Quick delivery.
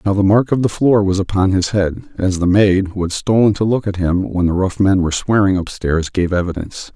Yes: fast, 250 wpm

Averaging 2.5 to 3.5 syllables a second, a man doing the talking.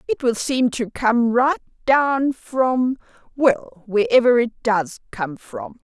No: 3.4 syllables/s; female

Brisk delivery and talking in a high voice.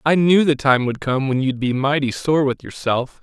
No: fast, 240 wpm; medium, 140 Hz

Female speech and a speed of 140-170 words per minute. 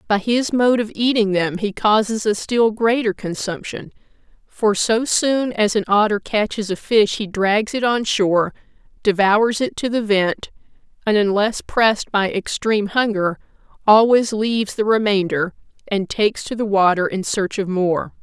Yes: female; average, 165 wpm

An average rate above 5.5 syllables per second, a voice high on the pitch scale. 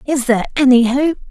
Yes: 6.1 syllables/s; very high, 260 Hz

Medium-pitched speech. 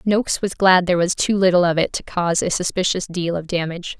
Yes: medium, 180 Hz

